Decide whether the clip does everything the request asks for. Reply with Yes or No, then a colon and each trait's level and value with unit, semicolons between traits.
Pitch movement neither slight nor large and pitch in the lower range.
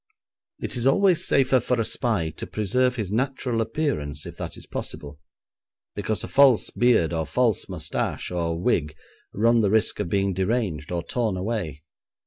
No: wide, 6.3 semitones; low, 110 Hz